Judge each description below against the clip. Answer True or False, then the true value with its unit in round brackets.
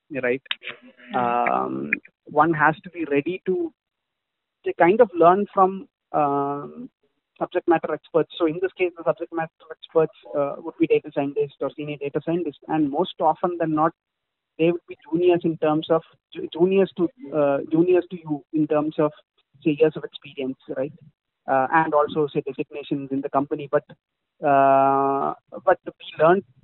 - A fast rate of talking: False (165 wpm)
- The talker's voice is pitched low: False (155 Hz)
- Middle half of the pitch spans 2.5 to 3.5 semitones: True (3.0 semitones)